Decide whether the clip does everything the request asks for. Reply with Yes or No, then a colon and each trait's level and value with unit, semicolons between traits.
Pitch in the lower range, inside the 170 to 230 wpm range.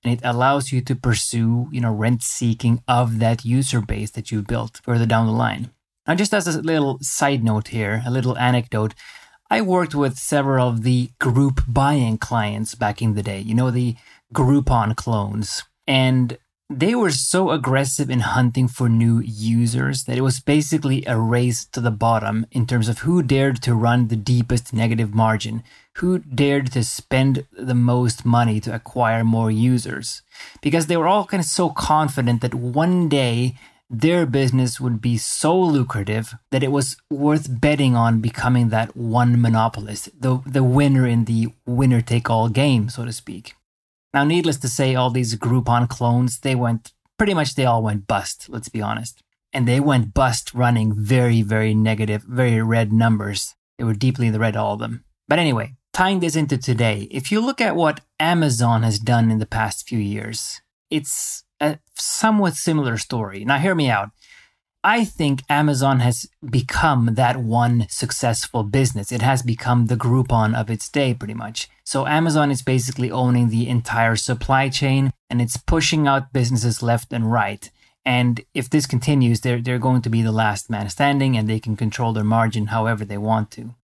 Yes: low, 120 Hz; average, 185 wpm